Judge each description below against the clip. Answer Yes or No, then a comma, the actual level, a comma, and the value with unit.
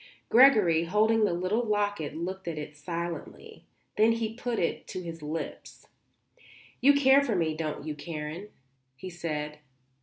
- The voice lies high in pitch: No, medium, 175 Hz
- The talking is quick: No, average, 150 wpm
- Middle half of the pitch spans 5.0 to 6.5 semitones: Yes, wide, 5.5 semitones